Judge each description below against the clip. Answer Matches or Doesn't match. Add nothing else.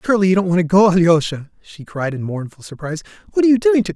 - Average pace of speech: Doesn't match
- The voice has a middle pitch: Matches